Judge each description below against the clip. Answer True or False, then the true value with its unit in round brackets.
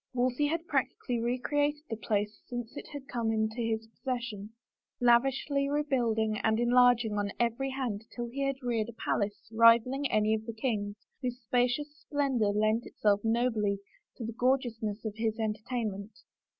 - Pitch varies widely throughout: False (2.7 semitones)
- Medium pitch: False (235 Hz)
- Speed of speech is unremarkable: True (160 wpm)